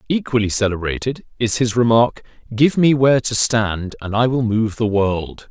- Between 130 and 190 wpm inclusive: Yes, average, 175 wpm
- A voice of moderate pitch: No, low, 115 Hz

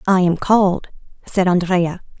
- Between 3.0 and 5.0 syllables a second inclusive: Yes, 4.5 syllables/s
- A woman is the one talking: Yes, female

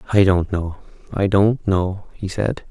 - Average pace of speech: Yes, average, 155 wpm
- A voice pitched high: No, very low, 95 Hz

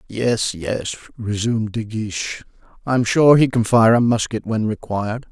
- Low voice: Yes, low, 110 Hz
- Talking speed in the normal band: Yes, average, 170 wpm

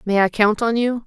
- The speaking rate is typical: No, fast, 280 wpm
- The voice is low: No, high, 220 Hz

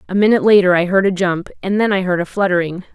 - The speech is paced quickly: Yes, fast, 265 wpm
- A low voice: No, high, 190 Hz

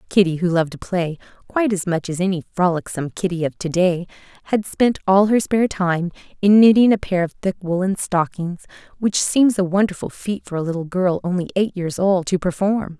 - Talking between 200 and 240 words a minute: Yes, fast, 205 wpm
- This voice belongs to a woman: Yes, female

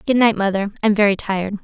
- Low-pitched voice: No, high, 205 Hz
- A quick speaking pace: Yes, fast, 220 wpm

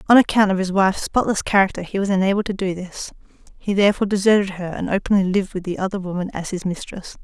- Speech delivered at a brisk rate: Yes, fast, 225 wpm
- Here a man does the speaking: No, female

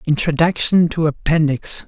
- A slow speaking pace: Yes, slow, 95 wpm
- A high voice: No, medium, 160 Hz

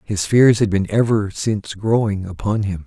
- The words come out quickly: No, average, 190 wpm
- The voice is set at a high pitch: No, low, 105 Hz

